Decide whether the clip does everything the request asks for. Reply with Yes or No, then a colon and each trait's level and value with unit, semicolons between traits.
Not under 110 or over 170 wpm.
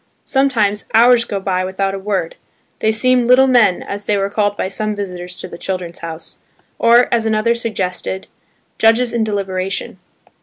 Yes: average, 165 wpm